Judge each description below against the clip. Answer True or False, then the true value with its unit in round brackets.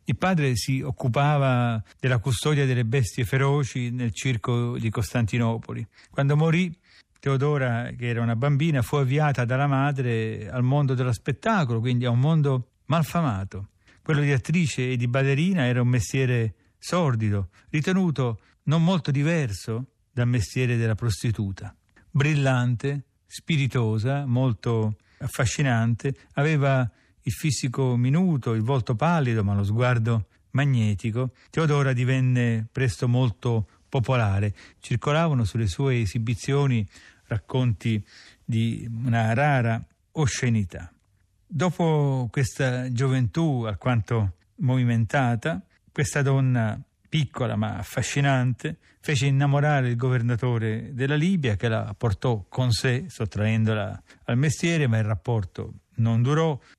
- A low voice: True (125 Hz)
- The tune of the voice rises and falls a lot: False (3.6 semitones)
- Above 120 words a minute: False (115 wpm)